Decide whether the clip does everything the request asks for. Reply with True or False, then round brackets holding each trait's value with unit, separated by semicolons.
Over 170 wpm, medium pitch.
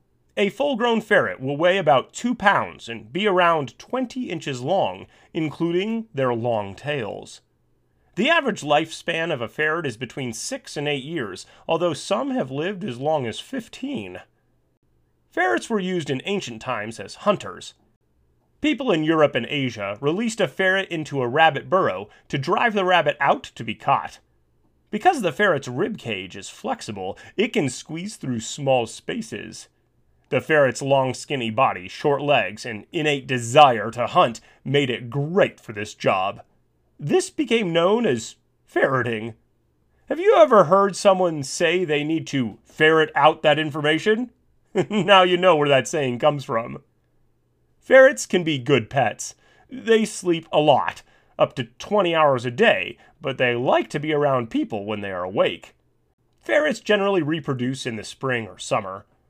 False (160 wpm; 155 Hz)